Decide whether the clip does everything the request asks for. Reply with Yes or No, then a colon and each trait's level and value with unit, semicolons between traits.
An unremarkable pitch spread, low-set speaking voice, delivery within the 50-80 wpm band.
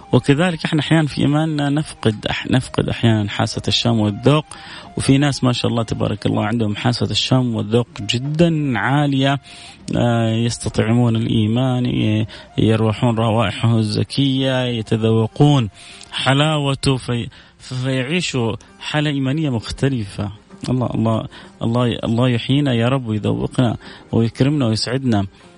No: average, 3.5 semitones; low, 120 Hz; average, 115 wpm